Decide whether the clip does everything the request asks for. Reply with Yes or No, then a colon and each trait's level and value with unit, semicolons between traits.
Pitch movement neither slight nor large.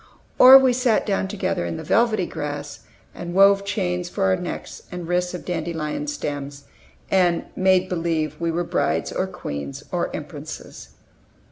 Yes: average, 3.6 semitones